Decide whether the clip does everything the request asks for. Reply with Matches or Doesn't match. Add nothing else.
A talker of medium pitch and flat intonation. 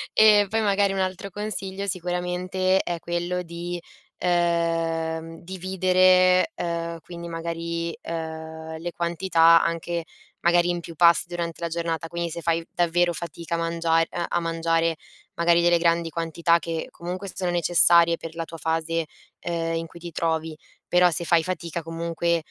Matches